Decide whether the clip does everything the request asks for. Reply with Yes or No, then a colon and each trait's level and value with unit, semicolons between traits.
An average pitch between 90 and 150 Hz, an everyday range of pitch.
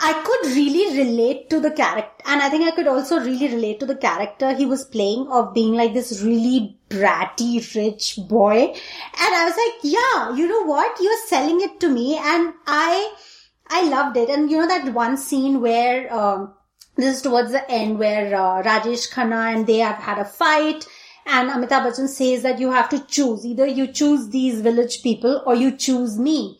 No: very high, 260 Hz; average, 4.5 semitones